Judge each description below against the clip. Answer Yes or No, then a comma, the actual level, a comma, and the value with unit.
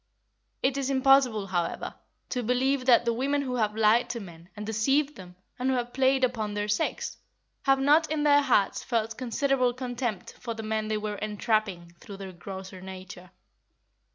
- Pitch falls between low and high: No, high, 230 Hz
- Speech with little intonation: No, average, 4.2 semitones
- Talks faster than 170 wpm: Yes, average, 180 wpm